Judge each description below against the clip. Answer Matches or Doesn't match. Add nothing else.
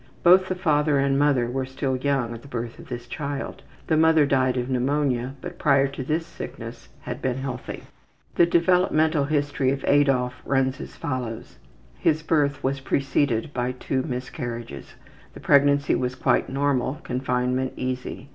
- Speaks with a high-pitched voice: Doesn't match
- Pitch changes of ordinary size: Doesn't match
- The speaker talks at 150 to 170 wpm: Matches